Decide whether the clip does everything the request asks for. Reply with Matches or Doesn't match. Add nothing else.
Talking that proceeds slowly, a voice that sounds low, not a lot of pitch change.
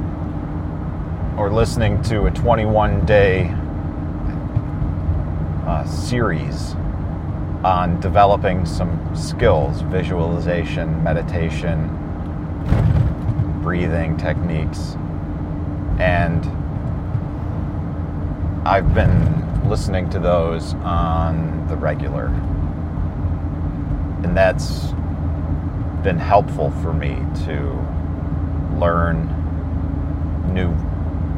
Matches